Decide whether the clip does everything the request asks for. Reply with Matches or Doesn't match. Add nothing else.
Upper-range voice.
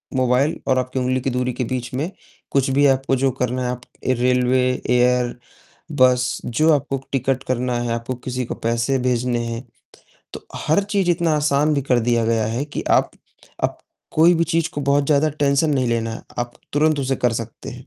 Doesn't match